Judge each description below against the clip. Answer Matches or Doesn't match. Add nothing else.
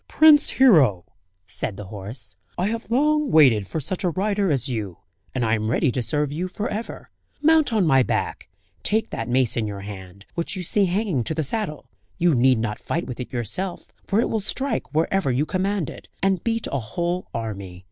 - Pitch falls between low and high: Matches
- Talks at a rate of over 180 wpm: Matches